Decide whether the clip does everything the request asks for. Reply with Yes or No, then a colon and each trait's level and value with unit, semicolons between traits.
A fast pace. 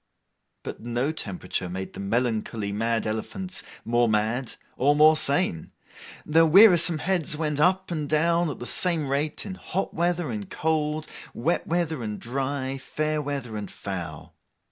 No: average, 150 wpm